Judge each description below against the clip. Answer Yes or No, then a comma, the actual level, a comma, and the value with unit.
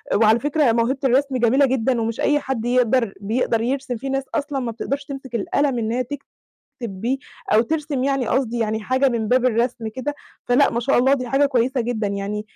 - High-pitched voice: Yes, very high, 250 Hz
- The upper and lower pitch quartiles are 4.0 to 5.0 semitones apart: No, average, 2.9 semitones